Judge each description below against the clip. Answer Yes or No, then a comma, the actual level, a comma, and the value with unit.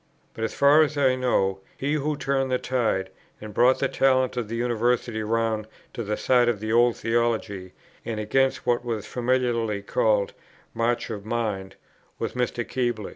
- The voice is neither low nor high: No, low, 120 Hz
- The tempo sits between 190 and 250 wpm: No, average, 175 wpm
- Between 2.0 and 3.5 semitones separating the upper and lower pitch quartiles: Yes, average, 2.9 semitones